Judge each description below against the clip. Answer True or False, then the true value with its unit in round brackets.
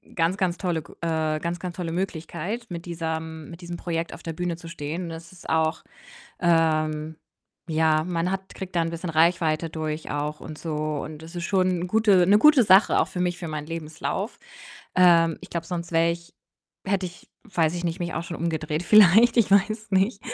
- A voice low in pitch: False (170 Hz)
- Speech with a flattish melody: True (2.3 semitones)